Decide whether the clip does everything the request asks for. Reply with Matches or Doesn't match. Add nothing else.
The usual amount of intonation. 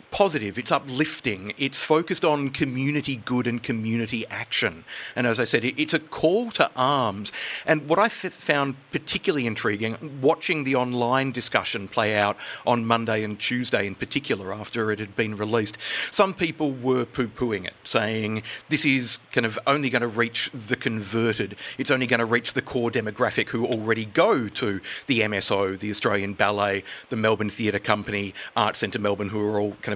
Matches